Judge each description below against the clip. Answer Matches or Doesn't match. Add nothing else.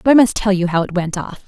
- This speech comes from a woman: Matches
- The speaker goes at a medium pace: Doesn't match